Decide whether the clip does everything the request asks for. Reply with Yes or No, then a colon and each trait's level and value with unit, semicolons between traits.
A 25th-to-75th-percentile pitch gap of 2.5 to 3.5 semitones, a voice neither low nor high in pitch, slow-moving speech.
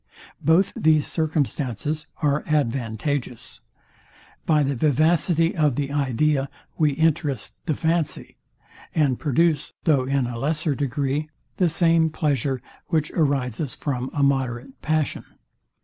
Yes: average, 2.8 semitones; medium, 145 Hz; slow, 115 wpm